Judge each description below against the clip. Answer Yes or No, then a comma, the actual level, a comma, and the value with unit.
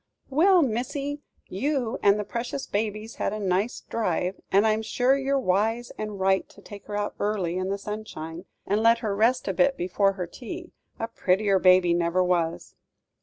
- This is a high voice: Yes, high, 210 Hz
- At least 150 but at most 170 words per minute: No, average, 180 wpm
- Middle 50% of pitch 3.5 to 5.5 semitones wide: Yes, average, 4.2 semitones